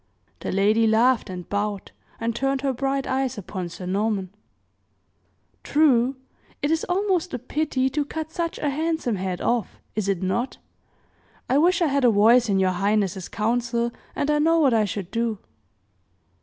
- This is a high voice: Yes, high, 235 Hz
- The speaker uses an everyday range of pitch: No, wide, 5.8 semitones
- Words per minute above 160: Yes, average, 170 wpm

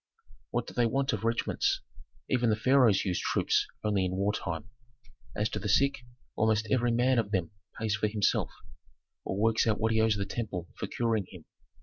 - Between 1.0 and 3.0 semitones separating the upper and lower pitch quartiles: Yes, narrow, 2.6 semitones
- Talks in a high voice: No, low, 110 Hz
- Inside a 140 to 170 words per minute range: No, average, 190 wpm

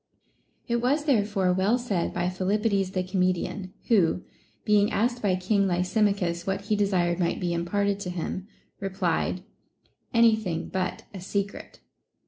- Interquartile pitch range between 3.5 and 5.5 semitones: No, narrow, 2.4 semitones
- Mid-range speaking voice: No, high, 195 Hz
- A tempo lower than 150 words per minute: Yes, average, 140 wpm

